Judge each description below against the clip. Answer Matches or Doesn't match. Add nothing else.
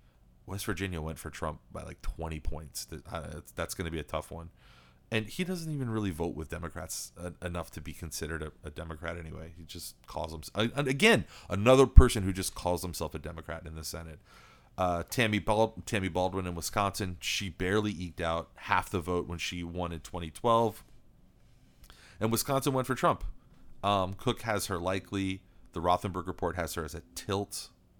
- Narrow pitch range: Doesn't match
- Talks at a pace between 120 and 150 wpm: Doesn't match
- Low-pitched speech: Matches